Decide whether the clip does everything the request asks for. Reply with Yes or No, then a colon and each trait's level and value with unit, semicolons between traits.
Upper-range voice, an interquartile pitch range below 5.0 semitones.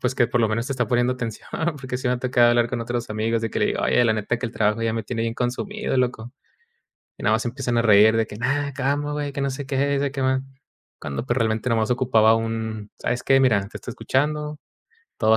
No: low, 120 Hz; average, 2.8 semitones